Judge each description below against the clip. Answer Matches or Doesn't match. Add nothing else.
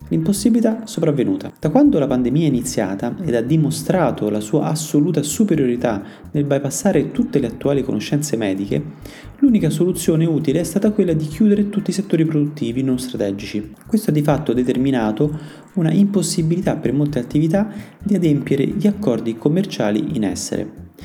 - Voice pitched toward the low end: Doesn't match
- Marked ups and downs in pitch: Matches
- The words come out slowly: Doesn't match